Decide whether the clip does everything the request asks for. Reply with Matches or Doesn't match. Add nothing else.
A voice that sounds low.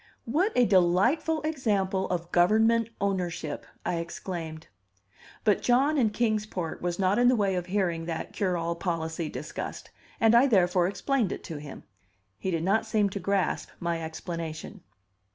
Doesn't match